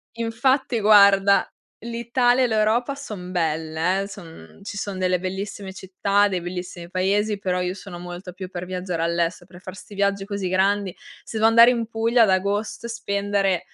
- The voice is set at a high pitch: Yes, high, 195 Hz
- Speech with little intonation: No, average, 3.0 semitones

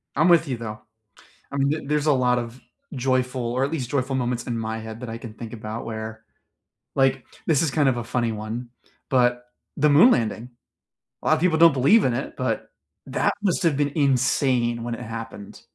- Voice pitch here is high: No, low, 125 Hz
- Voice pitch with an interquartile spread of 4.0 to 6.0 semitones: No, average, 3.5 semitones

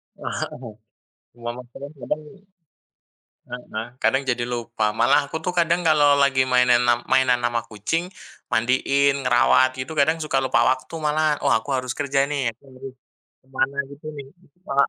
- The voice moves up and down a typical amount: Yes, average, 3.0 semitones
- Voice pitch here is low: Yes, low, 130 Hz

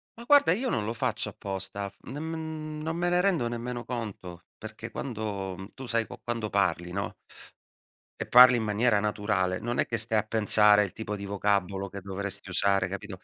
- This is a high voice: No, low, 105 Hz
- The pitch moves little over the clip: No, average, 3.8 semitones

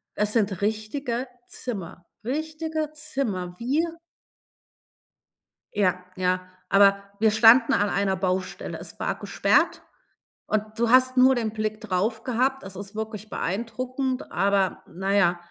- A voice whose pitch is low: No, high, 215 Hz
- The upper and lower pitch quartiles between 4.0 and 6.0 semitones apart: Yes, average, 4.6 semitones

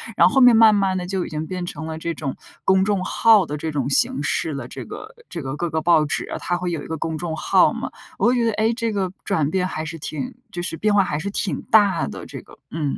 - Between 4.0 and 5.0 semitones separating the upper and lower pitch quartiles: Yes, average, 4.5 semitones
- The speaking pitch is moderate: Yes, medium, 175 Hz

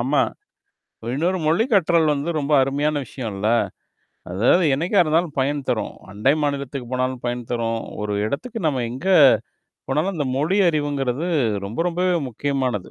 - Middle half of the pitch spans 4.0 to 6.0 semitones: Yes, average, 4.7 semitones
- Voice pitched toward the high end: No, medium, 140 Hz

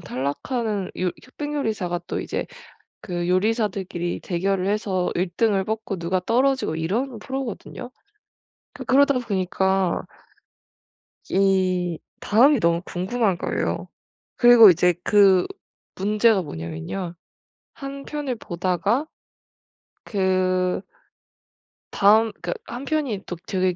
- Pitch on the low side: No, high, 195 Hz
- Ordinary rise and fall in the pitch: Yes, average, 4.4 semitones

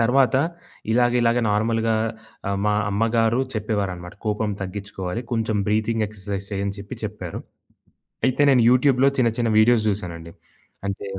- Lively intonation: No, average, 2.8 semitones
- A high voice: No, low, 110 Hz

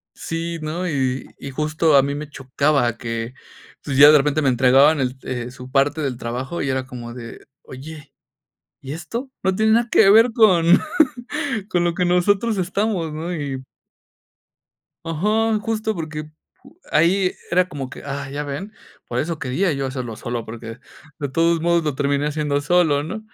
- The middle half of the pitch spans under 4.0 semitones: No, average, 4.7 semitones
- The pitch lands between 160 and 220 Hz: No, medium, 150 Hz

